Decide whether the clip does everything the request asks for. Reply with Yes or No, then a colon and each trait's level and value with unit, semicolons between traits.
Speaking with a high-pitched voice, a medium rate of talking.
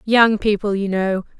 Yes: high, 205 Hz; average, 170 wpm